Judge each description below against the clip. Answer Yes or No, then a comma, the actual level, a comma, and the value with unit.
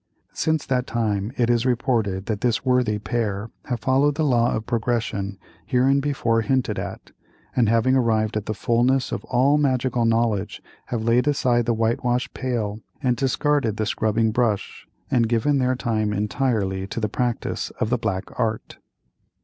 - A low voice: Yes, low, 120 Hz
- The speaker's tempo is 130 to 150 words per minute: No, average, 160 wpm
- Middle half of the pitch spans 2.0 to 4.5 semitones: Yes, average, 2.8 semitones